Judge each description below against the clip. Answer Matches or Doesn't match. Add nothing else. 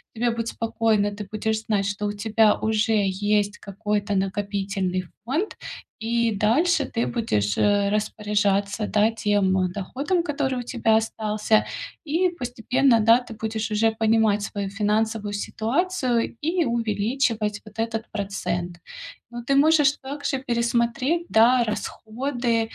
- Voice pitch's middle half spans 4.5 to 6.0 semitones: Doesn't match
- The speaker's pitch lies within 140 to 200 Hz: Doesn't match